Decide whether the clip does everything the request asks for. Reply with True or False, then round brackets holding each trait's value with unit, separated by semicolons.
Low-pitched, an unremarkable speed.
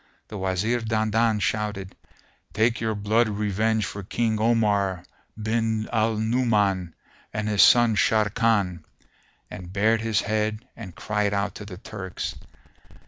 False (105 Hz; 130 wpm)